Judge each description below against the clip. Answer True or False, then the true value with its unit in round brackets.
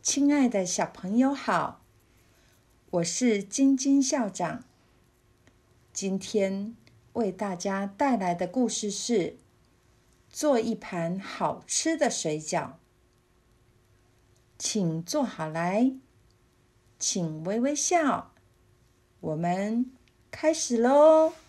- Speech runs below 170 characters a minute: True (125 characters per minute)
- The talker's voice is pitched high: True (195 Hz)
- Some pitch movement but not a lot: False (8.7 semitones)